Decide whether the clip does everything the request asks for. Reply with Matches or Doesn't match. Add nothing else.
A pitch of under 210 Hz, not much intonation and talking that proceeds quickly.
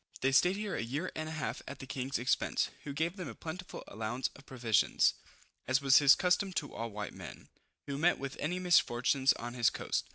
Doesn't match